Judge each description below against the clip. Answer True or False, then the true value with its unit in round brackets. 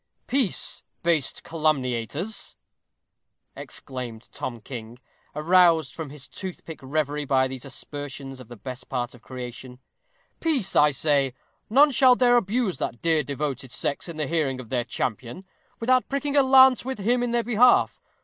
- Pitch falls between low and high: True (150 Hz)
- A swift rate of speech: False (155 wpm)